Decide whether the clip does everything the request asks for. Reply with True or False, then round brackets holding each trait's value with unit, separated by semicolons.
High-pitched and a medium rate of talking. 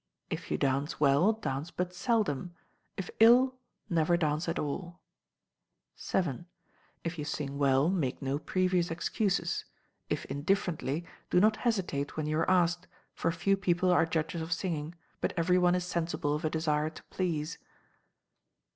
False (170 Hz; 155 wpm)